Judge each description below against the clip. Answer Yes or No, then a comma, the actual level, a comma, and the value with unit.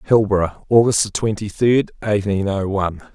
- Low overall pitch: Yes, low, 105 Hz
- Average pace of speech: Yes, average, 155 wpm